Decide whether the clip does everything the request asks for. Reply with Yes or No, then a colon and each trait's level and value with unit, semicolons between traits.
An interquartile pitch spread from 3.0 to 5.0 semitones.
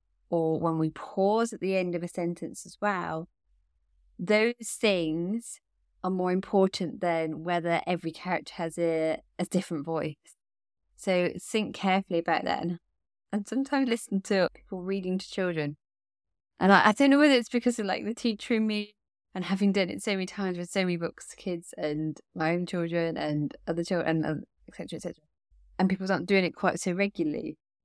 Yes: average, 3.5 semitones